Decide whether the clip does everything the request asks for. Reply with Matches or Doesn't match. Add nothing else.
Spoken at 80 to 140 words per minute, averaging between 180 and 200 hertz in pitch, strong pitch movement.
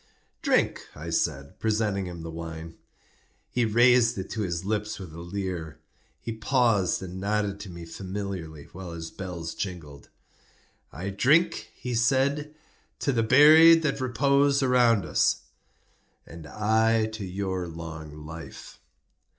Doesn't match